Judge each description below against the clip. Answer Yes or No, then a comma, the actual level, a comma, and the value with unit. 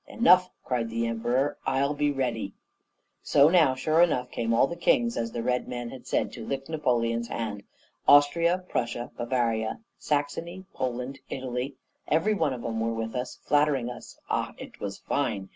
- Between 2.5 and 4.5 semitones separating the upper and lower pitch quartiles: Yes, average, 4.1 semitones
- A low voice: Yes, low, 130 Hz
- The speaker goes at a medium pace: Yes, average, 170 wpm